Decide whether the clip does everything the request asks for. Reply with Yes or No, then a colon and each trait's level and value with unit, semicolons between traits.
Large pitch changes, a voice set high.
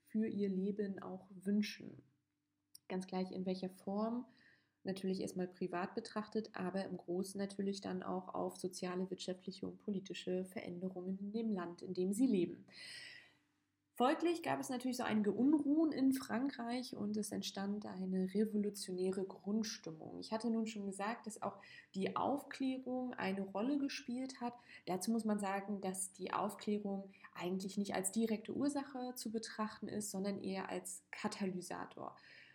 No: average, 3.5 semitones; high, 205 Hz